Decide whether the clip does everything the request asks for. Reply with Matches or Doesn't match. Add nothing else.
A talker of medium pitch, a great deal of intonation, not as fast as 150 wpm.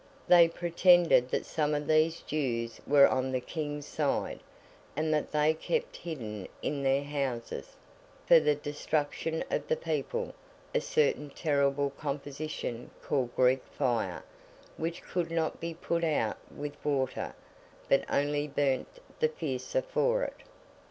Doesn't match